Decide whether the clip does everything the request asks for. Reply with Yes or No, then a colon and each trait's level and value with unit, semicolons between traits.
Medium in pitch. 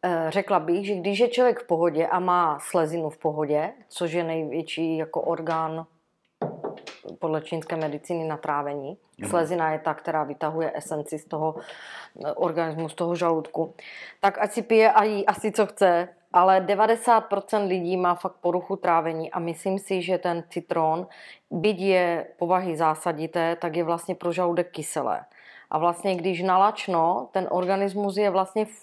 Yes: medium, 175 Hz